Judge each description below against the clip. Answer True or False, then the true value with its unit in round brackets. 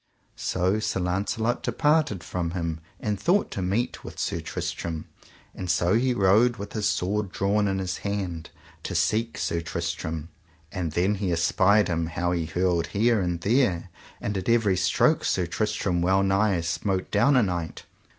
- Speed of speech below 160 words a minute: False (165 wpm)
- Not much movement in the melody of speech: False (3.5 semitones)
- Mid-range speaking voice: False (95 Hz)